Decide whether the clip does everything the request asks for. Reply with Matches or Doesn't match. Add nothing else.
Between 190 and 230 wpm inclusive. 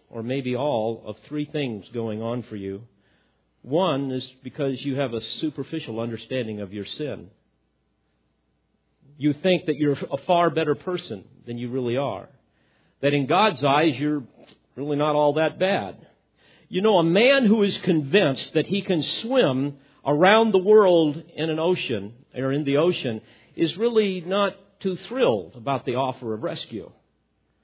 Doesn't match